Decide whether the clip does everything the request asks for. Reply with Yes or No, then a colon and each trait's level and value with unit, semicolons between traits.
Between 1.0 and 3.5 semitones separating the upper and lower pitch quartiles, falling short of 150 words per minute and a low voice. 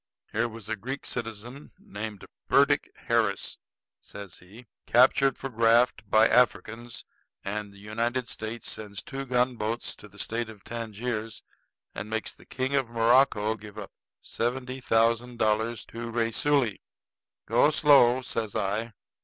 Yes: narrow, 2.4 semitones; average, 140 wpm; low, 115 Hz